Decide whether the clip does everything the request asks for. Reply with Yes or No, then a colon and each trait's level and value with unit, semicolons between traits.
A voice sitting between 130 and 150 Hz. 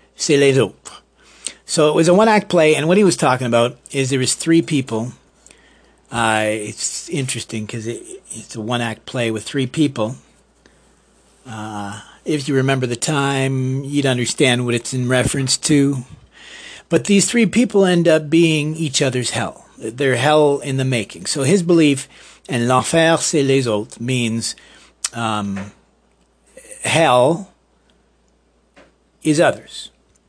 Yes: low, 135 Hz